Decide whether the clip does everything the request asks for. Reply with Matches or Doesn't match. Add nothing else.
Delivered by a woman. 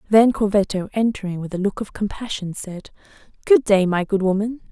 Matches